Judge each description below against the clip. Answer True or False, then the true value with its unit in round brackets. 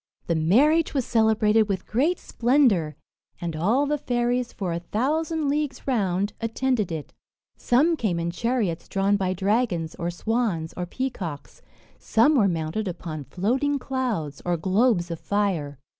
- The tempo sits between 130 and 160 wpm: True (145 wpm)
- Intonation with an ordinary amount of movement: False (6.7 semitones)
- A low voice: False (210 Hz)